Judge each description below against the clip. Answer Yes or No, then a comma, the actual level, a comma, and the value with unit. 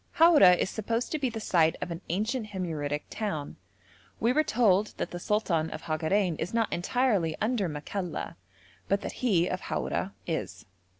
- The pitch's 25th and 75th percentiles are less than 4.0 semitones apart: No, average, 5.3 semitones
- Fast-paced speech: No, average, 170 wpm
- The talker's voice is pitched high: Yes, high, 195 Hz